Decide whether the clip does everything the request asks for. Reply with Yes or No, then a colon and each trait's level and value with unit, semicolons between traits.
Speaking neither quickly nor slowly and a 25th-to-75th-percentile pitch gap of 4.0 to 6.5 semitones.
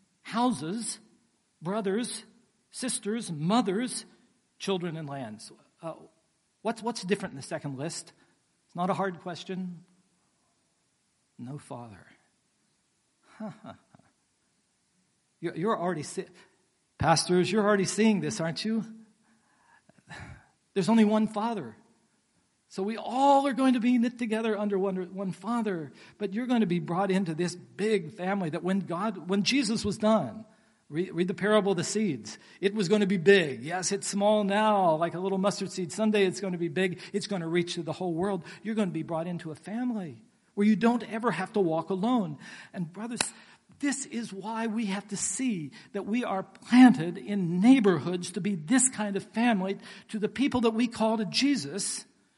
No: average, 170 wpm; average, 3.5 semitones